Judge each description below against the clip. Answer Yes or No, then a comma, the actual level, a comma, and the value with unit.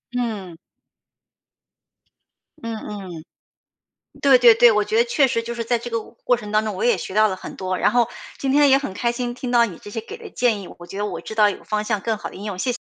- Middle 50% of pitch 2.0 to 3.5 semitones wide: Yes, average, 2.8 semitones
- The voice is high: Yes, high, 225 Hz